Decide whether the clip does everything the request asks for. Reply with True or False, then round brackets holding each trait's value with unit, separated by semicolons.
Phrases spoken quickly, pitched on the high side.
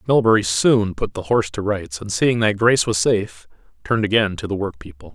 False (220 wpm; 105 Hz)